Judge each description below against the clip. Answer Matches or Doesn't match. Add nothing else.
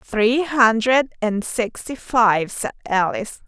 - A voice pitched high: Matches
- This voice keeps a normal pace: Doesn't match